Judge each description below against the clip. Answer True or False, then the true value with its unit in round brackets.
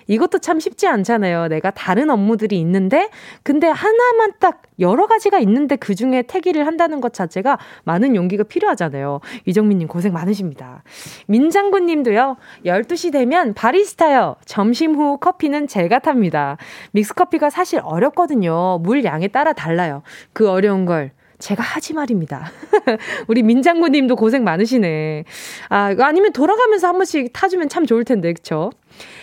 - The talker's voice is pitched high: True (245 Hz)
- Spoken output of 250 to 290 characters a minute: False (335 characters per minute)